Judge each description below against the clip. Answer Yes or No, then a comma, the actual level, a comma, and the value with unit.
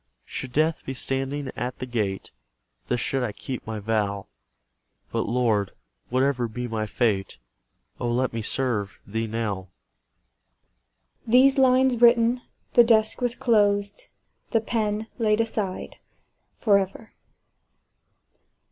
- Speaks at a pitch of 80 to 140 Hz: Yes, low, 135 Hz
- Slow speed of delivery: Yes, slow, 120 wpm